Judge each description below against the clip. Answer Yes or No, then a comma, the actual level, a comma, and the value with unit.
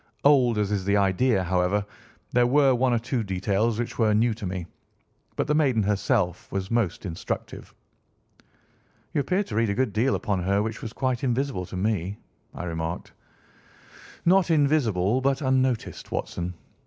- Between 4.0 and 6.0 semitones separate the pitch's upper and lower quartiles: Yes, average, 5.1 semitones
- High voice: No, low, 110 Hz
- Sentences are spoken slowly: No, average, 165 wpm